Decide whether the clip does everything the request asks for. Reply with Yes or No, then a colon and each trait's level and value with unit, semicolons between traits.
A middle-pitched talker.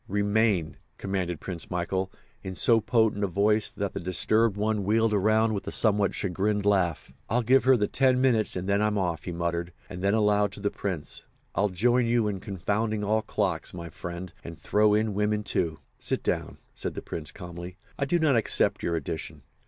No: low, 100 Hz